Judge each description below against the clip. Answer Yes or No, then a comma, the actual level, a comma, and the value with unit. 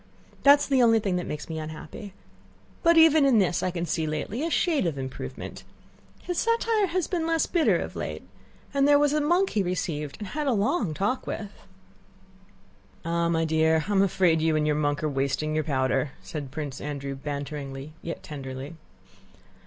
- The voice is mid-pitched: Yes, medium, 170 Hz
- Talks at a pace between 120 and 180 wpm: No, average, 190 wpm